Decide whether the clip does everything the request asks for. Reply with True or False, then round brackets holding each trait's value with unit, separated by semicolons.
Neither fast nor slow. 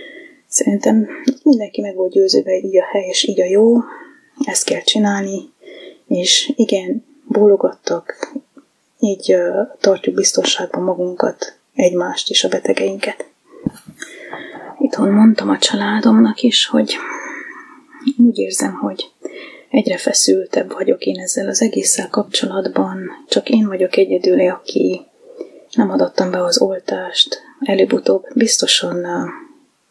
False (110 wpm)